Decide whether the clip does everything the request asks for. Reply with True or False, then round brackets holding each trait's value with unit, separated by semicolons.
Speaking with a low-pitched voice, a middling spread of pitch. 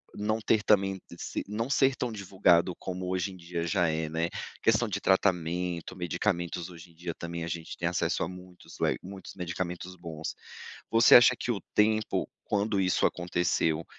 True (90 Hz; 3.2 semitones)